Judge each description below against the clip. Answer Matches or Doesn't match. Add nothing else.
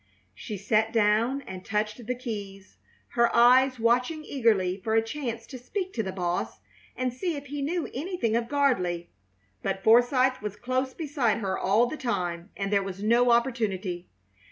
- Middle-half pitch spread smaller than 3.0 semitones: Doesn't match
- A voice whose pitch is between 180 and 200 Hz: Doesn't match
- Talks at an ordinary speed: Matches